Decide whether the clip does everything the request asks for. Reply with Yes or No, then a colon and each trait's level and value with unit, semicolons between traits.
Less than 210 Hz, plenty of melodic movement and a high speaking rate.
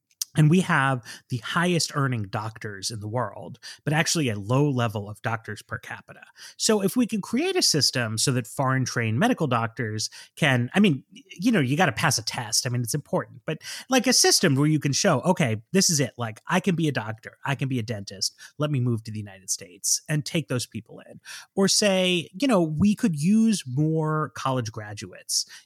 Yes: medium, 140 Hz; wide, 6.8 semitones; fast, 215 wpm